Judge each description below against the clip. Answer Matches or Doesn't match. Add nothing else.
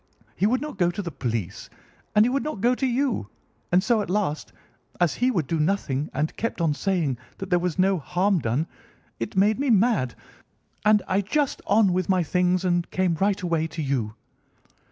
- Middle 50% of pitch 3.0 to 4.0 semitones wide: Doesn't match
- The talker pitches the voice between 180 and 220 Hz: Matches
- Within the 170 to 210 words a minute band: Matches